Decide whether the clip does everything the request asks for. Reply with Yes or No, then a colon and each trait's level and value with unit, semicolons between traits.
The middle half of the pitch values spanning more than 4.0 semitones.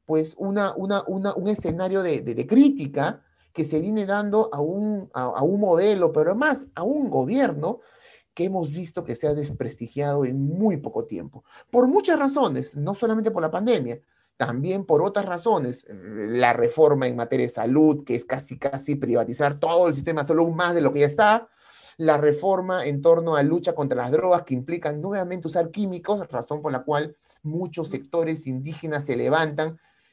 Yes: average, 5.1 semitones